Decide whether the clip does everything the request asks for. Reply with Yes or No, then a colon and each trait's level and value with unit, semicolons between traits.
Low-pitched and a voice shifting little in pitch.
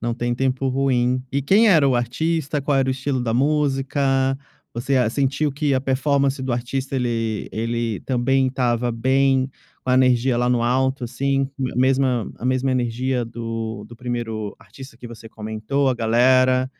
Yes: low, 130 Hz; narrow, 2.2 semitones